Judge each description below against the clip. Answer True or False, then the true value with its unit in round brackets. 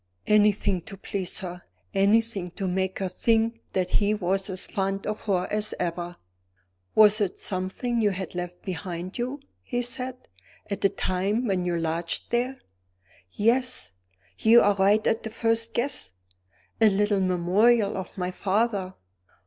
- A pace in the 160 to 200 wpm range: False (150 wpm)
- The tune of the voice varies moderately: True (3.4 semitones)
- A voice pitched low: False (200 Hz)